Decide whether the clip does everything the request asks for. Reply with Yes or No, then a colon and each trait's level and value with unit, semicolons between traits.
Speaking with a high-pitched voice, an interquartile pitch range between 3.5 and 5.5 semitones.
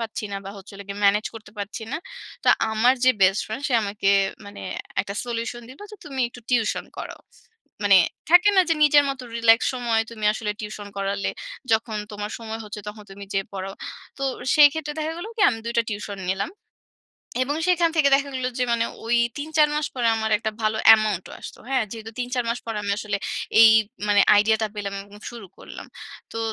Yes: high, 225 Hz; average, 3.8 semitones